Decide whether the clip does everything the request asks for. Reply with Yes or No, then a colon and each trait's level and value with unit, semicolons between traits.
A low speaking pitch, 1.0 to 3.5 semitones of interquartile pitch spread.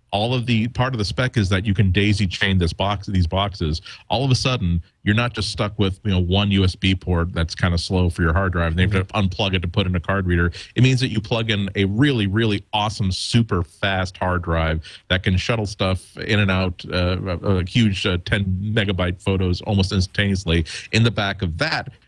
Yes: low, 100 Hz; average, 2.9 semitones